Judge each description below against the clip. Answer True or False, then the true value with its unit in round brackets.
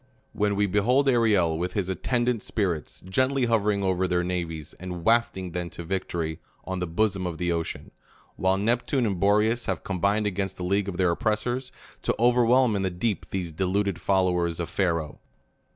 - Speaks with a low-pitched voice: True (95 Hz)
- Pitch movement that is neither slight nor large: True (3.6 semitones)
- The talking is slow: False (185 wpm)